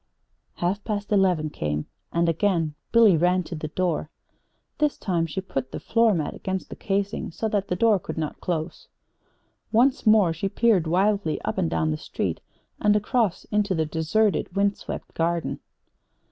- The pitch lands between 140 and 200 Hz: Yes, medium, 185 Hz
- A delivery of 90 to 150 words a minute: No, average, 170 wpm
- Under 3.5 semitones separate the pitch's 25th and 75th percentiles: No, average, 4.2 semitones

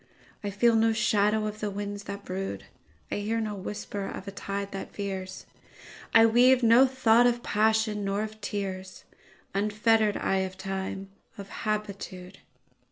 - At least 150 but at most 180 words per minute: No, average, 140 wpm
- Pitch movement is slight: Yes, narrow, 2.1 semitones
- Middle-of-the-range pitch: No, high, 205 Hz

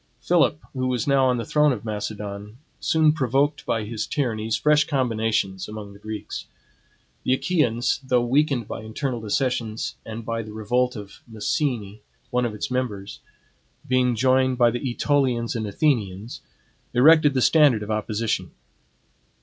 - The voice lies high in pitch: No, low, 120 Hz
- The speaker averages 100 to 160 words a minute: Yes, average, 150 wpm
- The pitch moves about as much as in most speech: Yes, average, 3.6 semitones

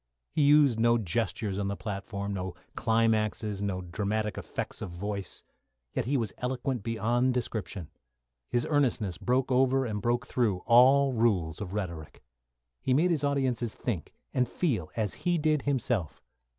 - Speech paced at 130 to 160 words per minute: Yes, average, 150 wpm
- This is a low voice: Yes, low, 115 Hz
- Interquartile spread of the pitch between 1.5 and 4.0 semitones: No, average, 4.5 semitones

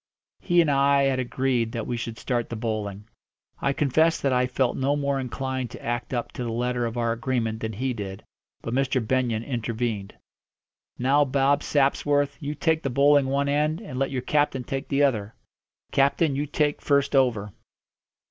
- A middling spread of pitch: Yes, average, 3.1 semitones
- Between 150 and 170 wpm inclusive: No, average, 185 wpm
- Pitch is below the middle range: Yes, low, 130 Hz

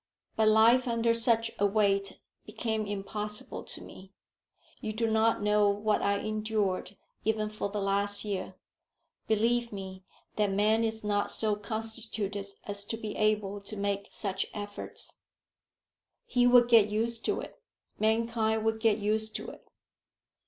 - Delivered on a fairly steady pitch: Yes, narrow, 1.6 semitones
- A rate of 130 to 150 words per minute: Yes, average, 145 wpm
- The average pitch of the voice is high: Yes, high, 215 Hz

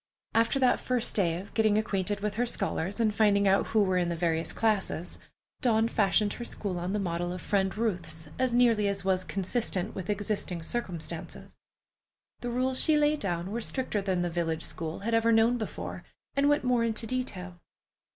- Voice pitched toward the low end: No, high, 205 Hz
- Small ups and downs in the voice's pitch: No, average, 4.4 semitones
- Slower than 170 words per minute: No, average, 190 wpm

